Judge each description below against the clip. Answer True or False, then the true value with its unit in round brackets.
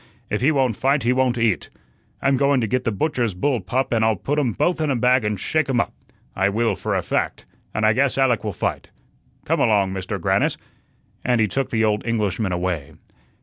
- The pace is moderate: False (220 wpm)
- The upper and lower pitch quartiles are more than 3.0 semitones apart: True (4.1 semitones)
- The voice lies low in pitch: True (115 Hz)